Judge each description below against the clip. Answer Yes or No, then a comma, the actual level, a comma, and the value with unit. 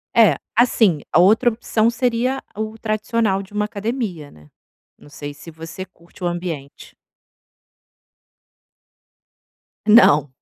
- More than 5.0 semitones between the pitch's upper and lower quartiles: Yes, wide, 5.6 semitones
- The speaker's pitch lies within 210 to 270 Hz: No, high, 200 Hz